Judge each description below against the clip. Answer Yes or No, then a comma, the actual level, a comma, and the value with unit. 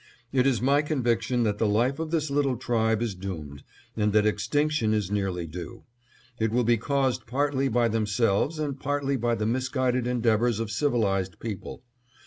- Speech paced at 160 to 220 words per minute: Yes, average, 170 wpm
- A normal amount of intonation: Yes, average, 4.2 semitones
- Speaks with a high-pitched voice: No, low, 120 Hz